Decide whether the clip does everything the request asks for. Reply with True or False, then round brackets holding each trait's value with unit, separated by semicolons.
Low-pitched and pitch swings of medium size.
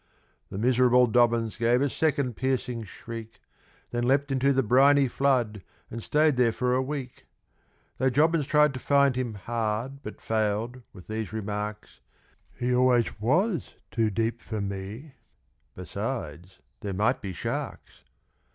True (120 Hz; 3.5 semitones)